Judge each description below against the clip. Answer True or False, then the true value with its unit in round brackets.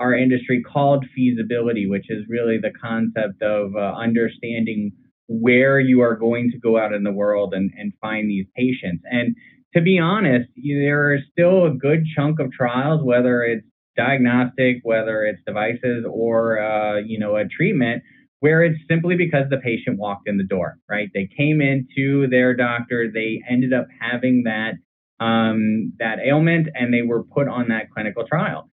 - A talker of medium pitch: False (120 Hz)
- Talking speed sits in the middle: True (175 wpm)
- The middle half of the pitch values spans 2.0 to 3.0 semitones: False (3.4 semitones)